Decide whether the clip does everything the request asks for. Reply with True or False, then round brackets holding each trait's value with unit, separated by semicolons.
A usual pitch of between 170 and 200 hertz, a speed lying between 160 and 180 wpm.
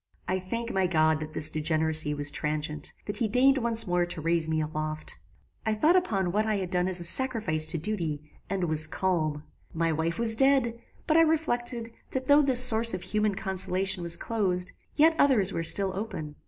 False (185 Hz; 195 wpm)